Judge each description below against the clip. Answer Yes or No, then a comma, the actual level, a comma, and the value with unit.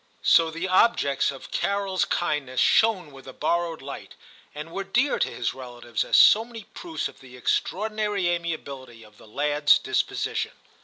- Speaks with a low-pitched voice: No, medium, 165 Hz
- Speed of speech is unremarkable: Yes, average, 160 wpm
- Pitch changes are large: Yes, wide, 6.7 semitones